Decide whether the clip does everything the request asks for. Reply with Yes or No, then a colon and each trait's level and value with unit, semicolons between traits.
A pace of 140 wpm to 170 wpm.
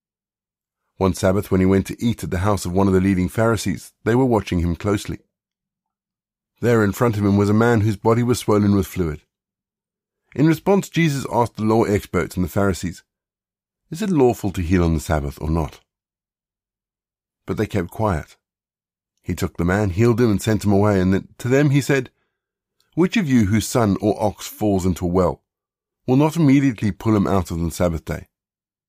No: average, 195 wpm